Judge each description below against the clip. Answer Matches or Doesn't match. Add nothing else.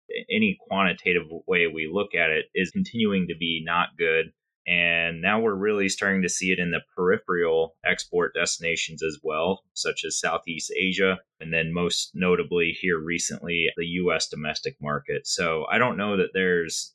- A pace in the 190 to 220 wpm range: Doesn't match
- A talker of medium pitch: Doesn't match